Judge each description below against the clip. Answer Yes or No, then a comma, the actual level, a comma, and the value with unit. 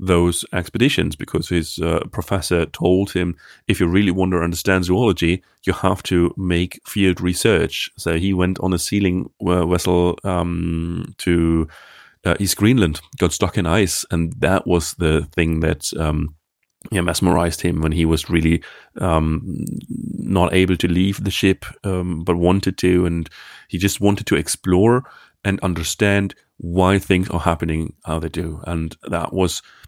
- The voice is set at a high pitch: No, very low, 90 Hz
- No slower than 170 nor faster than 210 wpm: No, average, 160 wpm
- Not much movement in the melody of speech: Yes, narrow, 2.1 semitones